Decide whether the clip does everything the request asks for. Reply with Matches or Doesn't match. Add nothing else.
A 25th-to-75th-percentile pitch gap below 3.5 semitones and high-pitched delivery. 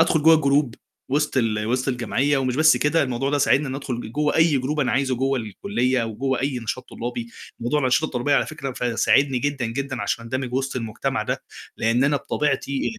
Doesn't match